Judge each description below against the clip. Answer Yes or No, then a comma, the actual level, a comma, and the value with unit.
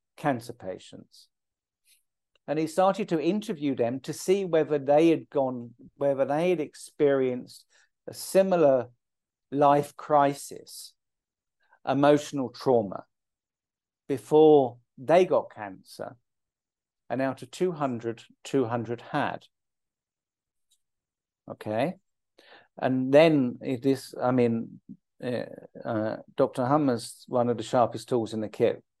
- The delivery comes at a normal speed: No, slow, 105 wpm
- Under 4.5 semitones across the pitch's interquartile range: Yes, average, 3.7 semitones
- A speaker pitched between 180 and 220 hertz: No, low, 135 Hz